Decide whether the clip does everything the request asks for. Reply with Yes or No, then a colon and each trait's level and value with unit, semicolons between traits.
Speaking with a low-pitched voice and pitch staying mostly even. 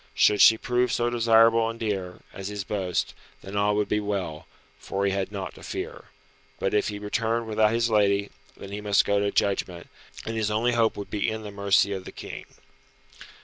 Yes: low, 105 Hz; narrow, 2.1 semitones